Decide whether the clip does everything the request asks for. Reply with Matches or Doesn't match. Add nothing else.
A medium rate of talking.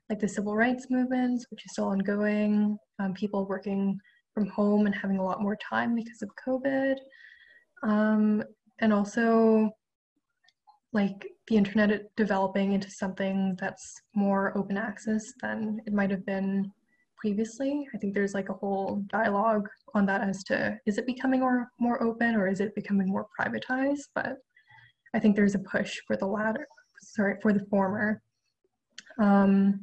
Matches